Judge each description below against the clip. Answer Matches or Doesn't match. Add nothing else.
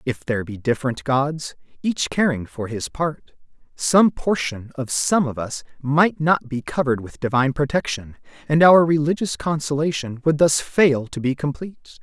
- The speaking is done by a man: Matches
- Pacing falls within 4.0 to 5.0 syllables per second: Matches